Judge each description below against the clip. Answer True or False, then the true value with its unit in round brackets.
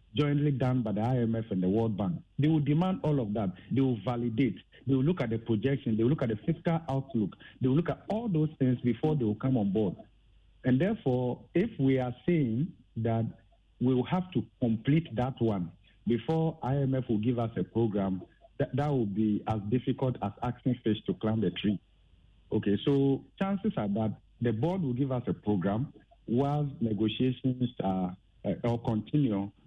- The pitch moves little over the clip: False (4.3 semitones)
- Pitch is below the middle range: True (125 Hz)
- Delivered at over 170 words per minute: True (195 wpm)